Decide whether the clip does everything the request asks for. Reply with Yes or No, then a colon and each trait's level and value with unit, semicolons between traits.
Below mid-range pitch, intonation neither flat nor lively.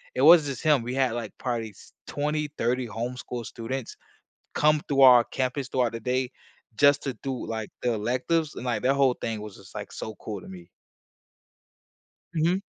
Yes: low, 125 Hz; average, 3.3 semitones